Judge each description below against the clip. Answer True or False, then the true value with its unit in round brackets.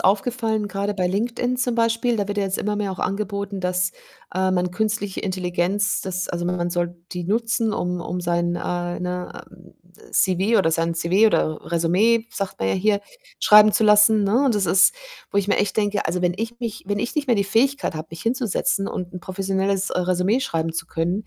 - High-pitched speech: True (195 Hz)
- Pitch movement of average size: True (3.2 semitones)